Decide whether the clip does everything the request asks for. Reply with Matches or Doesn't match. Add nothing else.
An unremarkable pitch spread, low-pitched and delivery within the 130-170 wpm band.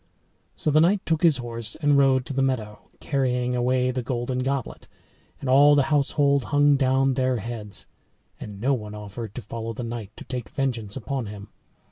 Doesn't match